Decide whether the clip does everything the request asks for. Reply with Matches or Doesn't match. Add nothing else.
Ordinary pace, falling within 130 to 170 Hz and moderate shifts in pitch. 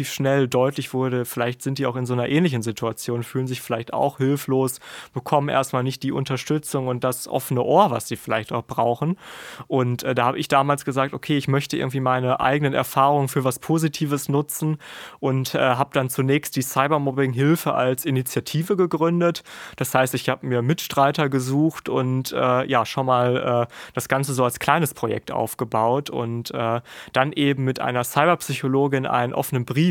Doesn't match